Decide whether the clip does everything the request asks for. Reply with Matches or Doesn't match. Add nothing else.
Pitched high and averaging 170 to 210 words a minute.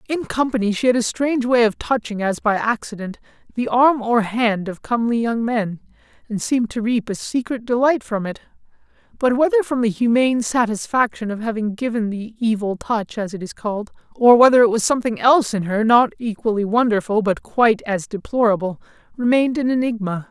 Matches